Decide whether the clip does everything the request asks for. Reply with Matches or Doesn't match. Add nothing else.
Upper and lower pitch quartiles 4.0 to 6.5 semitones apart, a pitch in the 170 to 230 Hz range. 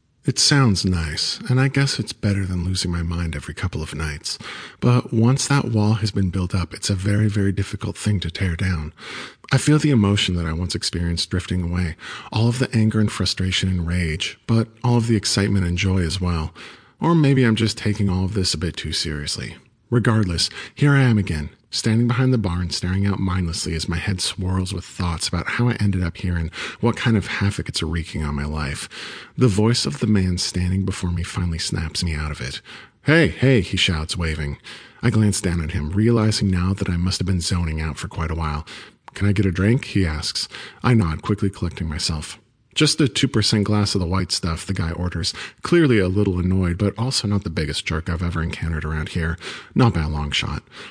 Doesn't match